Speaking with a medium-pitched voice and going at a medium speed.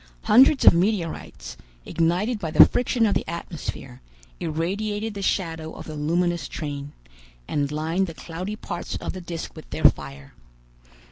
Yes: medium, 170 Hz; average, 150 wpm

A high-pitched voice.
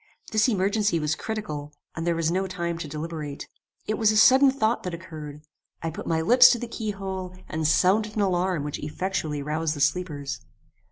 No: medium, 175 Hz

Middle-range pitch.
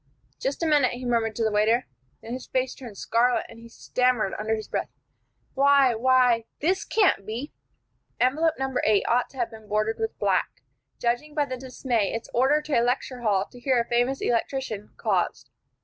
No: high, 245 Hz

